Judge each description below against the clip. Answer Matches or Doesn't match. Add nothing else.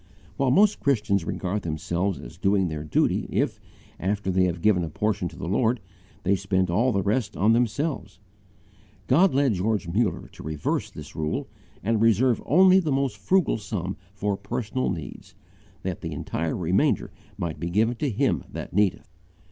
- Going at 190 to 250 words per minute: Doesn't match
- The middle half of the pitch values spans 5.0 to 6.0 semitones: Matches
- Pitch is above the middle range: Doesn't match